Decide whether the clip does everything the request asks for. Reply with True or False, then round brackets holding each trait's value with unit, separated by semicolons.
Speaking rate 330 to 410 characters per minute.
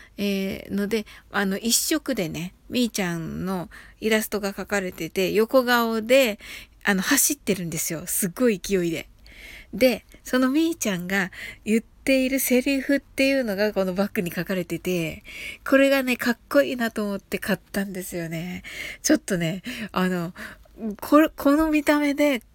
False (310 characters per minute)